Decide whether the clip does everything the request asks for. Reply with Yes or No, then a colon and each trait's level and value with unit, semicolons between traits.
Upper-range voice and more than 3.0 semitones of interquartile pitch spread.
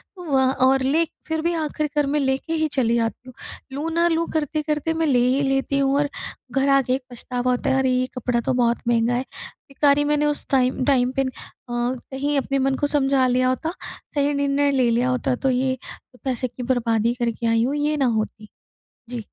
No: very high, 265 Hz; average, 2.7 semitones